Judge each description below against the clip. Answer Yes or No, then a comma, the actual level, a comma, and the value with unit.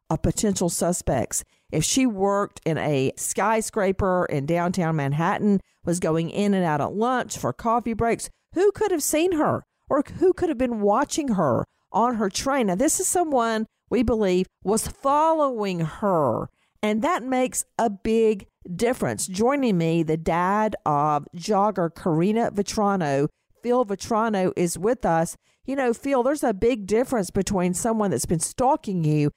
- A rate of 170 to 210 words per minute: No, average, 160 wpm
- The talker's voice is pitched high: Yes, high, 205 Hz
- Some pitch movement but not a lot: No, wide, 5.8 semitones